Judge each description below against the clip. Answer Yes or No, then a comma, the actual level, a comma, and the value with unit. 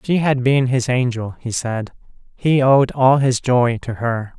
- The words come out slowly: No, average, 190 wpm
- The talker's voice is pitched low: Yes, low, 125 Hz